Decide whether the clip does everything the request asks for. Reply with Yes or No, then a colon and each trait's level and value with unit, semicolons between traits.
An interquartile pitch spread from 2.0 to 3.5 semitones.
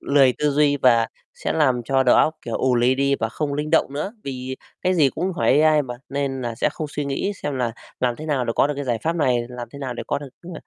Yes: average, 2.9 semitones